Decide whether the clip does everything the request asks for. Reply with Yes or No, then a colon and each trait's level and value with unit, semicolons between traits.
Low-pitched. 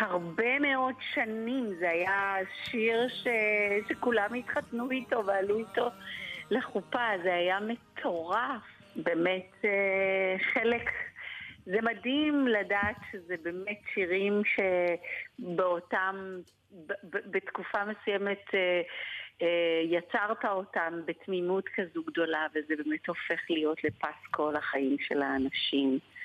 No: high, 195 Hz